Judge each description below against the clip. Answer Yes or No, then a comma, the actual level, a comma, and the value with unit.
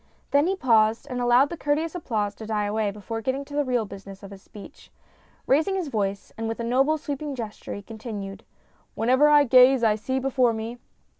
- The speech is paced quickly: Yes, fast, 210 wpm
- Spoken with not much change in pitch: No, average, 4.5 semitones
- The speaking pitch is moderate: No, high, 240 Hz